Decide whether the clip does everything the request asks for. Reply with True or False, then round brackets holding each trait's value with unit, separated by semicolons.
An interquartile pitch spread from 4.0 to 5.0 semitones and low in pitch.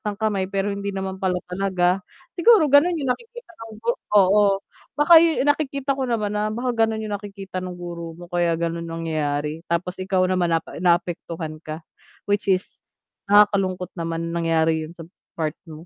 False (4.4 semitones; 190 Hz)